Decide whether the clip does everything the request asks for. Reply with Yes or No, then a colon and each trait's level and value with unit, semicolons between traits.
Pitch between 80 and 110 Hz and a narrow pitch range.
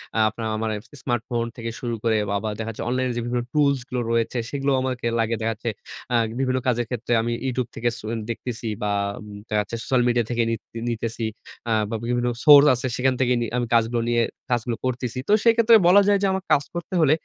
No: low, 120 Hz; narrow, 2.1 semitones